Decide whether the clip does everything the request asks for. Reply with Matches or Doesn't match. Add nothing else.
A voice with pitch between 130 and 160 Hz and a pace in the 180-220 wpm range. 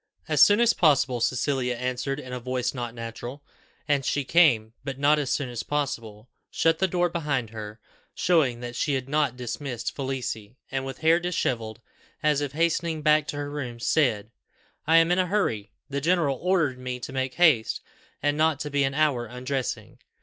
Matches